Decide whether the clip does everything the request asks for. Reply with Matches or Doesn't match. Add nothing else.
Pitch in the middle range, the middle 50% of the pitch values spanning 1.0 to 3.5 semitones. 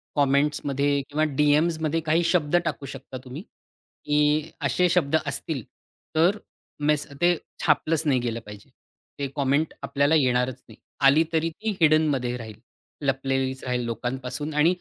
Matches